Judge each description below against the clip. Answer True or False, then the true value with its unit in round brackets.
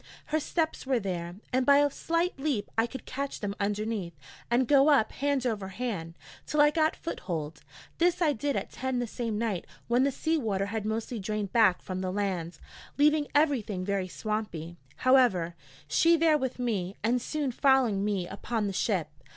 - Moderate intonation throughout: False (6.0 semitones)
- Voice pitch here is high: True (230 Hz)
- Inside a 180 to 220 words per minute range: True (185 wpm)